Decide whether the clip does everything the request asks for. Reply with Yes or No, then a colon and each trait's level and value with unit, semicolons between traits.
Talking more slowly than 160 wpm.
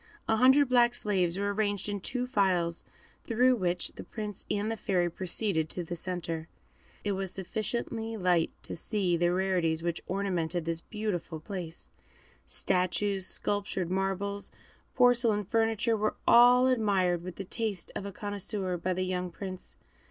Yes: average, 150 wpm